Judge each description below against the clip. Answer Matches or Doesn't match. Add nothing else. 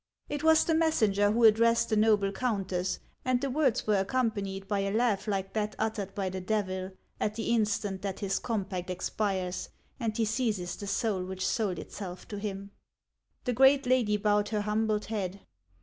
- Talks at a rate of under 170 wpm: Doesn't match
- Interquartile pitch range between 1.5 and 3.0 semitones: Matches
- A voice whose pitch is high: Matches